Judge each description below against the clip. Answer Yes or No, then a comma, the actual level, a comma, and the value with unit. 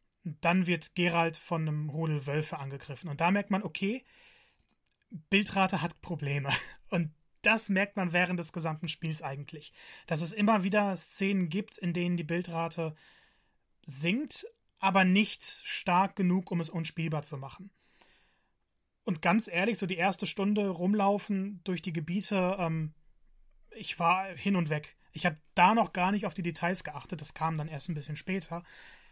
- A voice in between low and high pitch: Yes, medium, 175 Hz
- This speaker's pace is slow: No, average, 160 wpm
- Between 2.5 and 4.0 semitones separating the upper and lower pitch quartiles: Yes, average, 3.2 semitones